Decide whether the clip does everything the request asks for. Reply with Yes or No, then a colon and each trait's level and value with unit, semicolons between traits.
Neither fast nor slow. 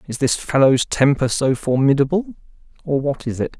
Yes: average, 165 wpm